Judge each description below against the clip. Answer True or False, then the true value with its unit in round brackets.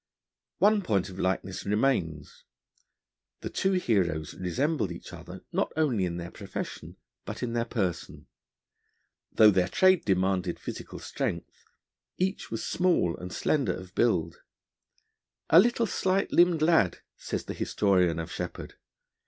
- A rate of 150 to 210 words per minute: False (135 wpm)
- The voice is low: True (100 Hz)